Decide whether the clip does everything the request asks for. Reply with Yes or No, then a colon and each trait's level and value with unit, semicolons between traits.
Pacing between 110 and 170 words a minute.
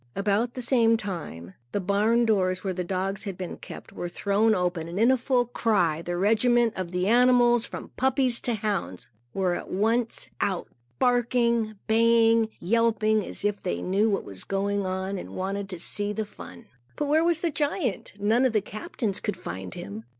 No: average, 185 wpm